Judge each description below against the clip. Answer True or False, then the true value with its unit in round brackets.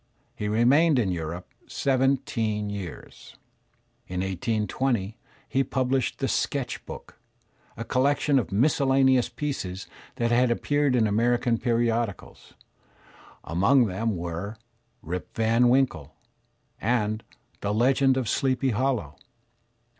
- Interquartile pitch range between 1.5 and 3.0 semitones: False (4.4 semitones)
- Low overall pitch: True (115 Hz)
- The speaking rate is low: True (110 wpm)